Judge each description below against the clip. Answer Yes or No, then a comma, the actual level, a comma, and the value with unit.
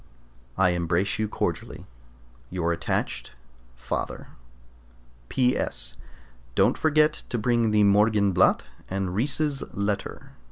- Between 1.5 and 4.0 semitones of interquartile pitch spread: No, average, 4.7 semitones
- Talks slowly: Yes, slow, 95 wpm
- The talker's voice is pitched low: Yes, low, 100 Hz